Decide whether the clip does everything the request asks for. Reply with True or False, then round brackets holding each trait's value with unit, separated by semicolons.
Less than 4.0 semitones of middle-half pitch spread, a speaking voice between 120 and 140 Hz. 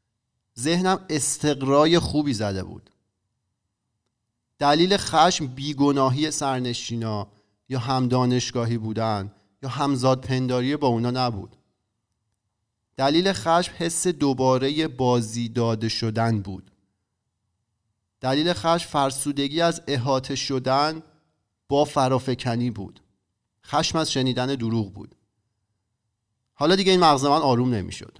False (4.6 semitones; 125 Hz)